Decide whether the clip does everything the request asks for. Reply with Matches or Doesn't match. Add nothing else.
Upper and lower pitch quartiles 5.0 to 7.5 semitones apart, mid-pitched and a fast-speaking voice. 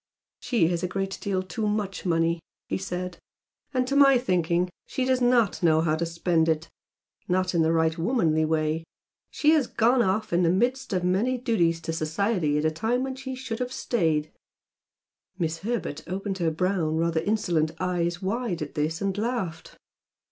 Doesn't match